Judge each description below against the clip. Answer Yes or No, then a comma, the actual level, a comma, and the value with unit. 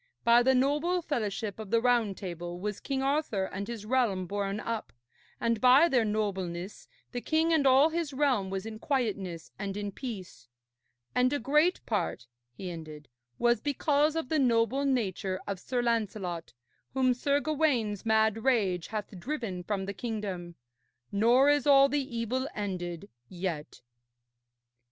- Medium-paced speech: Yes, average, 155 wpm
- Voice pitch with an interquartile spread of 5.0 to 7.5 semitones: Yes, wide, 5.5 semitones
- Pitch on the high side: Yes, high, 225 Hz